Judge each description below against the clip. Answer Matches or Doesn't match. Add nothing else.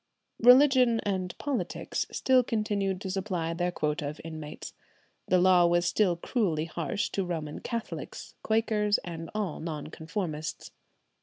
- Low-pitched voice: Doesn't match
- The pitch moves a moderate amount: Matches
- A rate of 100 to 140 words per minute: Matches